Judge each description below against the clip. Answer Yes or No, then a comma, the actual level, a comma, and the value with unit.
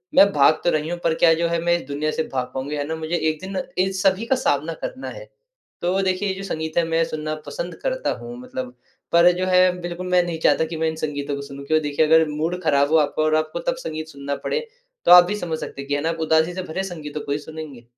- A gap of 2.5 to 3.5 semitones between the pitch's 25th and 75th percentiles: Yes, average, 3.0 semitones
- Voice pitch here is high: No, medium, 160 Hz